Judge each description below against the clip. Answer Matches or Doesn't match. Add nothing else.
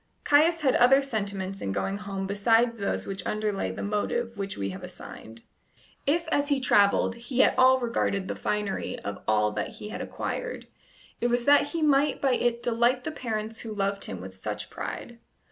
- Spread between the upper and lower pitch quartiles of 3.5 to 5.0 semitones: Matches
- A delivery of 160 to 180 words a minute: Doesn't match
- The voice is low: Doesn't match